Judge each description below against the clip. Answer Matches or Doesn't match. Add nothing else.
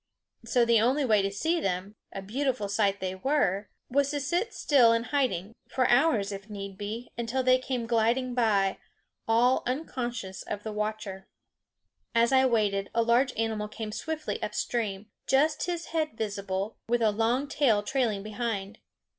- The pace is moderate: Matches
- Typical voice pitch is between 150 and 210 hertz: Doesn't match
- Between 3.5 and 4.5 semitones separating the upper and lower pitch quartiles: Matches